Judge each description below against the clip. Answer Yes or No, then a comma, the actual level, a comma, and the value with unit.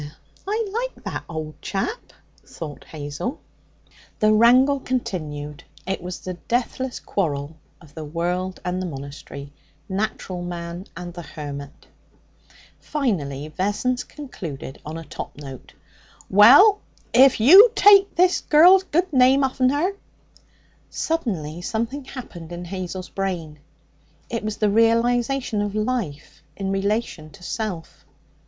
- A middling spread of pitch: No, wide, 7.9 semitones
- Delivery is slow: Yes, slow, 130 wpm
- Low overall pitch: No, high, 195 Hz